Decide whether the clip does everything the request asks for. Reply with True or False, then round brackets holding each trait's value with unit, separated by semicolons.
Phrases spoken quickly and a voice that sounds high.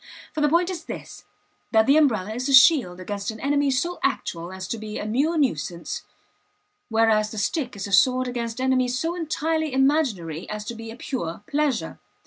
False (190 wpm; 250 Hz)